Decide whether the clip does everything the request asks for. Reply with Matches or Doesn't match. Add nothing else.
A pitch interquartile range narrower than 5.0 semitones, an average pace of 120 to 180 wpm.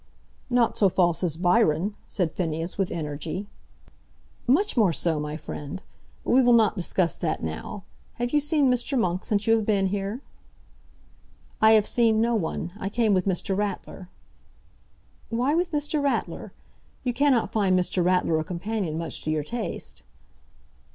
Doesn't match